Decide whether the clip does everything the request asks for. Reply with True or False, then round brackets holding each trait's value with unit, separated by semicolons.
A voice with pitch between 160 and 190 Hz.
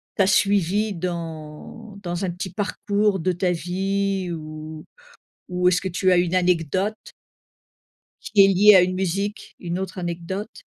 True (185 Hz)